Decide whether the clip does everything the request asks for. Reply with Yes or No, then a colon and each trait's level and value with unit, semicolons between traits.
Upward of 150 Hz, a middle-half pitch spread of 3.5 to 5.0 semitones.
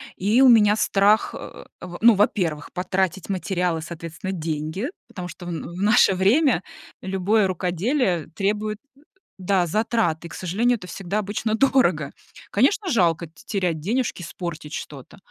Yes: high, 190 Hz; average, 3.8 semitones